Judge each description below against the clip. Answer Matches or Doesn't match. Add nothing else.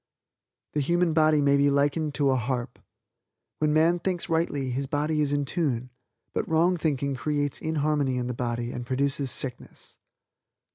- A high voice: Doesn't match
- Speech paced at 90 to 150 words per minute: Doesn't match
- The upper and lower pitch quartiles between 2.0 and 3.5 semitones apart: Matches